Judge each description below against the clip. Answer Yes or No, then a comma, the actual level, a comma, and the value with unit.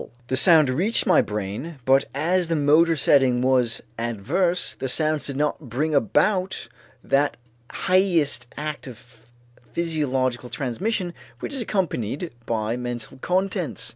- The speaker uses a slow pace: Yes, slow, 130 wpm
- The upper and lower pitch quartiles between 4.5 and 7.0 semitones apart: Yes, wide, 5.5 semitones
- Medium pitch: Yes, medium, 145 Hz